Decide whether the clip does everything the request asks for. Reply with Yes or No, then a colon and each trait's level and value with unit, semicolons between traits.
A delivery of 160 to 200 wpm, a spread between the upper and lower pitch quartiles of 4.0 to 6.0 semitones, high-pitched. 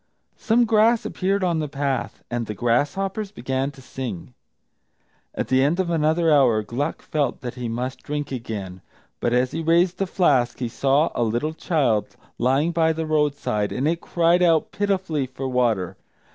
No: average, 175 wpm; wide, 5.4 semitones; medium, 145 Hz